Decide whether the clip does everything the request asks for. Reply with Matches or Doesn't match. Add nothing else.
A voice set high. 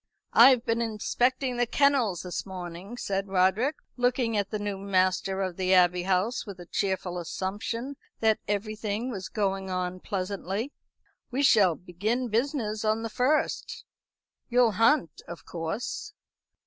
Matches